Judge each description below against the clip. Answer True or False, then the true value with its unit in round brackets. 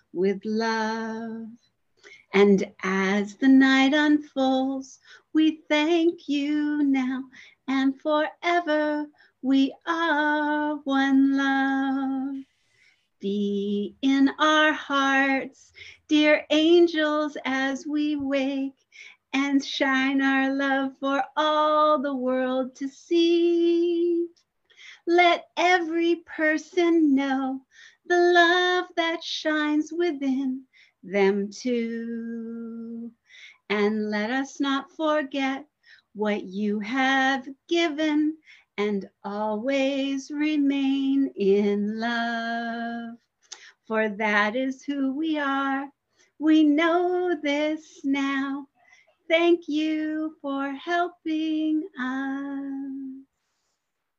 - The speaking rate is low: True (85 wpm)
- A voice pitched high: True (275 Hz)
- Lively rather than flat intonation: False (3.0 semitones)